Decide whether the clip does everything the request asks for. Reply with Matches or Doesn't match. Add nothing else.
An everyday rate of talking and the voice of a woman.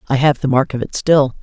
Doesn't match